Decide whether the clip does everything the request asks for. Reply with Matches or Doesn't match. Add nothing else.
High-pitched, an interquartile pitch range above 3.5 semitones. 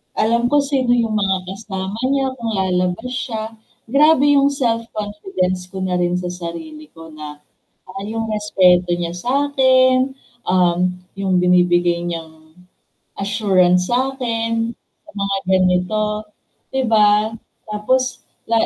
Matches